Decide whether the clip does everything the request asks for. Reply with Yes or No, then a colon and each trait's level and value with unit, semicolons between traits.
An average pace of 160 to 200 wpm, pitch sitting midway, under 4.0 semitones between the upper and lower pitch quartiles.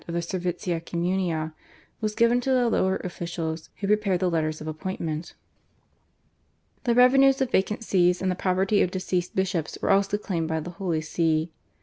Yes: average, 175 wpm; medium, 180 Hz; average, 3.2 semitones